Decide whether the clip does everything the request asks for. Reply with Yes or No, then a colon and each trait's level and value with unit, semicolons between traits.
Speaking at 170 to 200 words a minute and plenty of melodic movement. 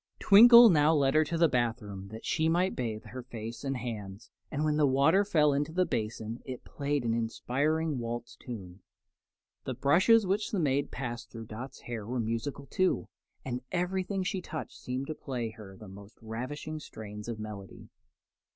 Yes: average, 185 wpm; wide, 5.8 semitones